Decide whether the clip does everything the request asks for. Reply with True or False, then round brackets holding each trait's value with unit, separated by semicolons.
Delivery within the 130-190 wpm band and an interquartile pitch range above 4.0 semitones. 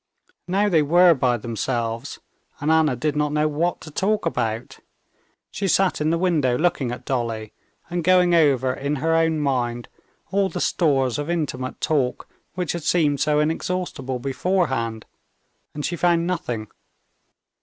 True (155 wpm; 5.2 semitones)